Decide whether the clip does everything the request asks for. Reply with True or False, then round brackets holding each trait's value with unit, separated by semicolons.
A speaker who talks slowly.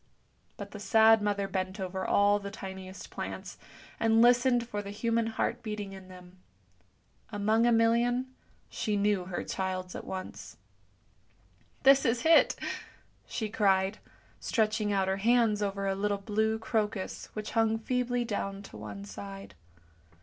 False (150 wpm)